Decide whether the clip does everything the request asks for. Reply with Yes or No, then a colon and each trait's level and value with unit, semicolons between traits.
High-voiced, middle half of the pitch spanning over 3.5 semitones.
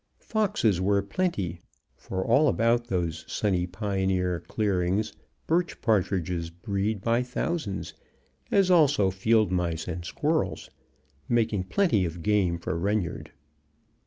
No: low, 100 Hz; average, 4.5 semitones